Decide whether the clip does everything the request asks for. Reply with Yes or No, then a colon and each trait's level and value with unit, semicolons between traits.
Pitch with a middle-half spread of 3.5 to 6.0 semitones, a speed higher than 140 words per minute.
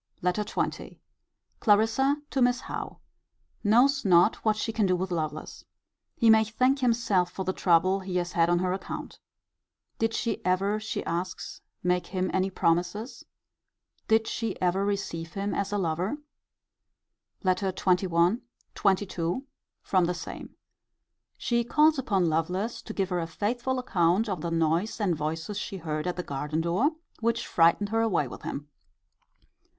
Yes: average, 4.2 semitones; average, 155 wpm